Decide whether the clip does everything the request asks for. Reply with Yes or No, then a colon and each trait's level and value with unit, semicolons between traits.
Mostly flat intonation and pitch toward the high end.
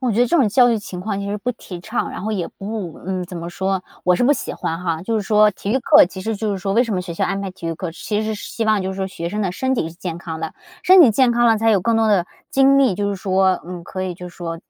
No: average, 3.8 semitones; high, 200 Hz